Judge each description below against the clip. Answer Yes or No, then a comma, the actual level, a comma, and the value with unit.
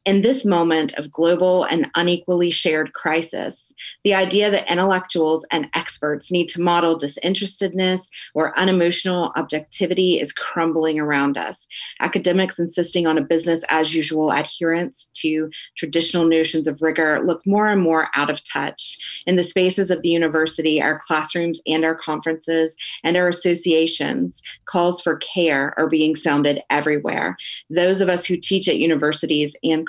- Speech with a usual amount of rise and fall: No, narrow, 2.2 semitones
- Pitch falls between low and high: Yes, medium, 165 Hz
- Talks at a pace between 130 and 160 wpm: Yes, average, 150 wpm